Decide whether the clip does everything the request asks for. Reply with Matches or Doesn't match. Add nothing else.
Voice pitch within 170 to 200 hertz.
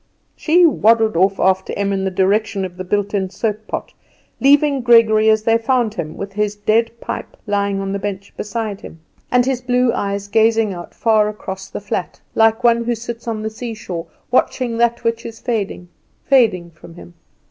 Doesn't match